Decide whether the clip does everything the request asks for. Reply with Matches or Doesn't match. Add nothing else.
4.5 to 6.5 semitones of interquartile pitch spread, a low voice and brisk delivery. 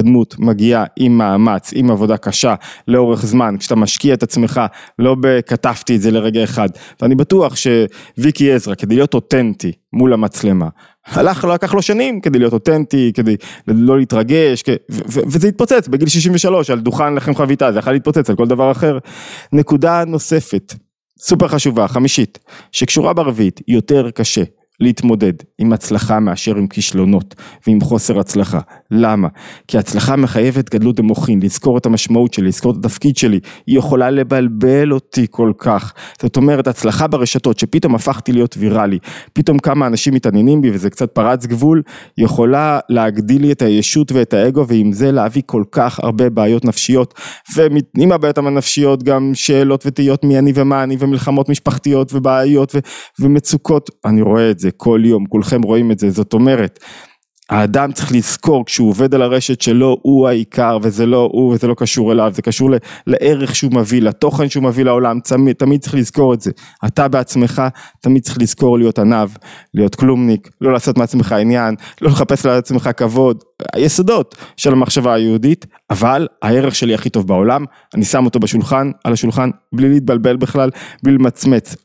Doesn't match